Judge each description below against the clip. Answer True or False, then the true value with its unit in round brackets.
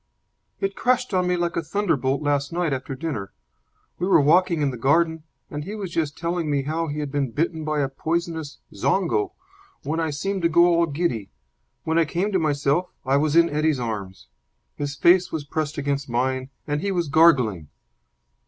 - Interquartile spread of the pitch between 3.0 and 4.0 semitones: True (3.4 semitones)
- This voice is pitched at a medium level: True (155 Hz)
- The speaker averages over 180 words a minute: True (190 wpm)